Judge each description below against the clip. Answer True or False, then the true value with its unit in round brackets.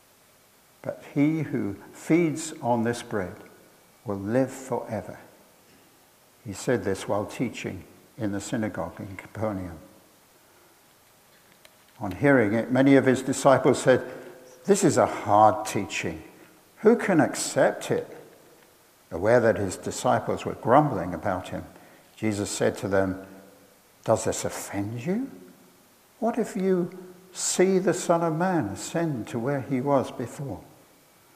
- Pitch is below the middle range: True (125 Hz)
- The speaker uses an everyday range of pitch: False (7.6 semitones)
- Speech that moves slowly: True (130 wpm)